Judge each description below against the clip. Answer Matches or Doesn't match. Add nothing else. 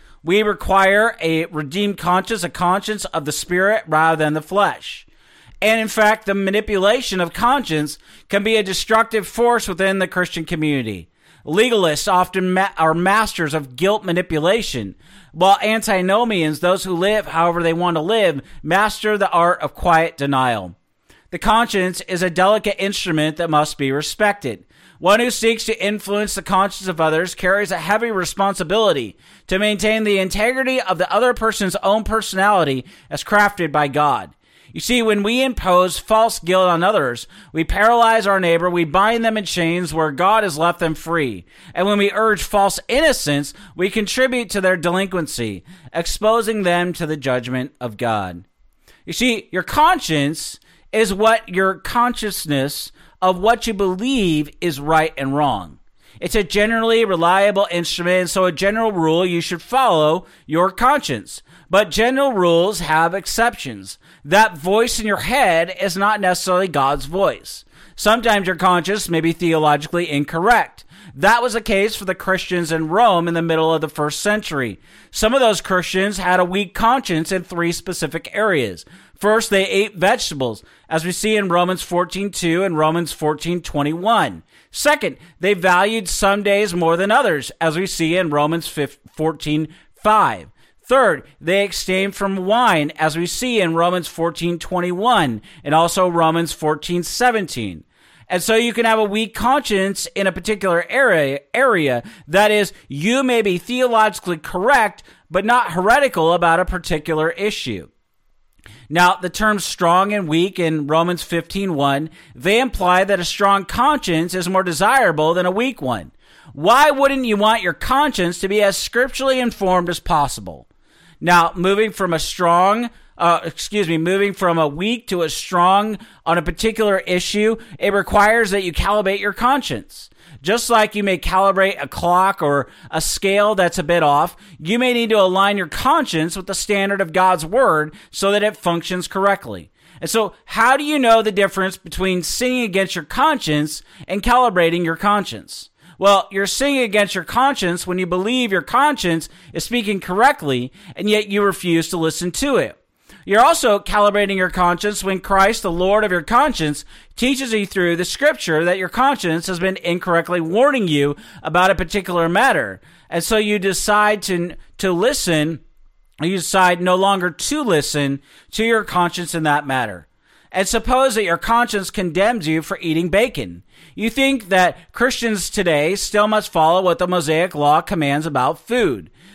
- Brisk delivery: Doesn't match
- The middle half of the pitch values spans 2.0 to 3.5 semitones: Doesn't match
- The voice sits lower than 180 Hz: Doesn't match